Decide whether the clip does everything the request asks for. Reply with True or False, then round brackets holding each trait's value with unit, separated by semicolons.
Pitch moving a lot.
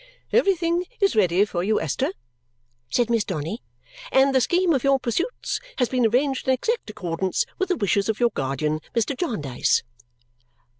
True (7.4 semitones)